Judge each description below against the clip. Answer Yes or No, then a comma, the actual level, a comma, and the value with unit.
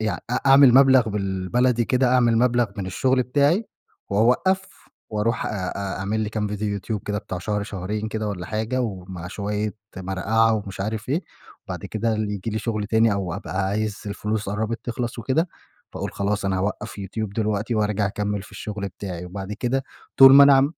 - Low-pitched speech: Yes, low, 105 Hz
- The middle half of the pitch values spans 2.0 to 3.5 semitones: Yes, average, 2.9 semitones